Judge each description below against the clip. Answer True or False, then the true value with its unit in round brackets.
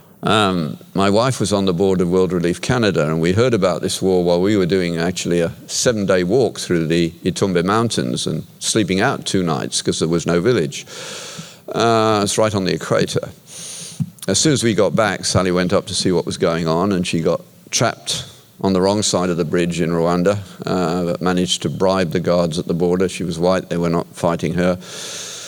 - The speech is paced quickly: True (215 wpm)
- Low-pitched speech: True (90 Hz)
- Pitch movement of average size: False (2.0 semitones)